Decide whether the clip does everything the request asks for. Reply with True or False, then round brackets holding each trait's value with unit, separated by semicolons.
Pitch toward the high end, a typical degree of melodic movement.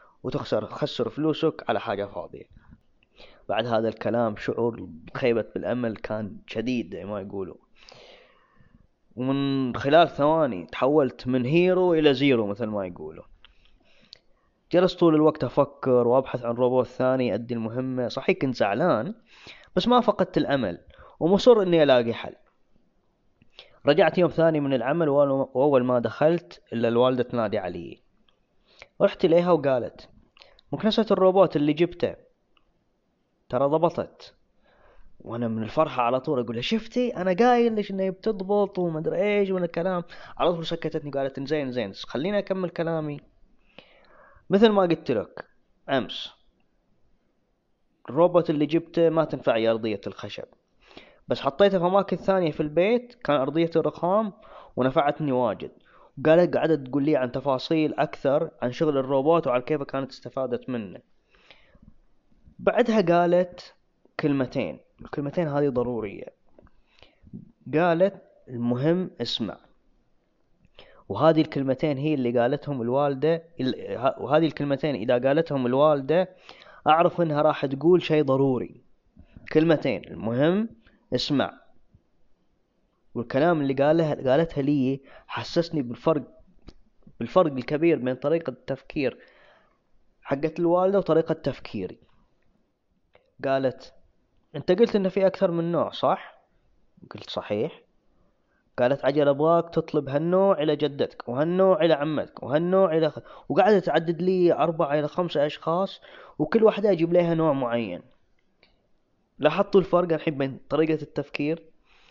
False (150 Hz; 5.0 semitones)